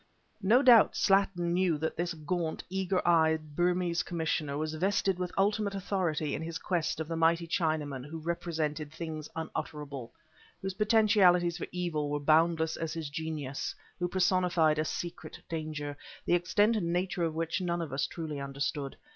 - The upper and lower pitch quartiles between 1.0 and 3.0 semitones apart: Yes, narrow, 2.6 semitones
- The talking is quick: No, average, 165 wpm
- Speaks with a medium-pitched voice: Yes, medium, 165 Hz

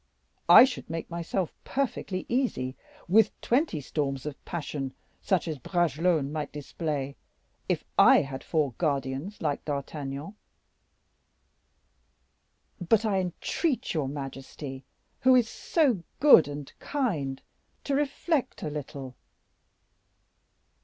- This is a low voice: No, medium, 160 Hz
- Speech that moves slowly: Yes, slow, 110 wpm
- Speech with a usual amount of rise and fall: No, wide, 7.0 semitones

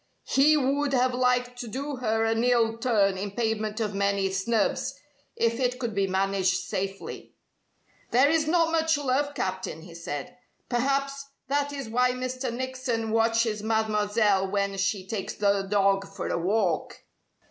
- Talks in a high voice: Yes, high, 225 Hz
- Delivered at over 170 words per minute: No, average, 155 wpm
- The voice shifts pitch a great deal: No, average, 4.5 semitones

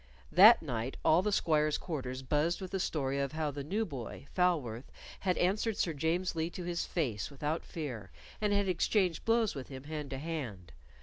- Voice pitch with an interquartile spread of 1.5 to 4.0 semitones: No, average, 4.9 semitones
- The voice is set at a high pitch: No, medium, 155 Hz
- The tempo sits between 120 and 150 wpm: No, average, 190 wpm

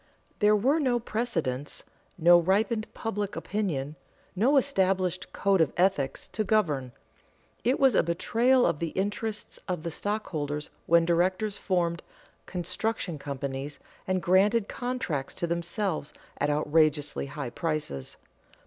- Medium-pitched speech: Yes, medium, 180 Hz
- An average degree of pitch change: No, wide, 5.7 semitones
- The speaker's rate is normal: No, slow, 125 wpm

